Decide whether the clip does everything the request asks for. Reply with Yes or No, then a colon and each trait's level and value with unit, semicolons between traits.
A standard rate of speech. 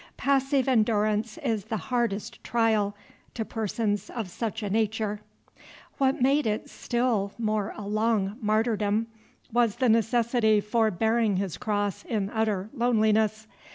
No: slow, 130 wpm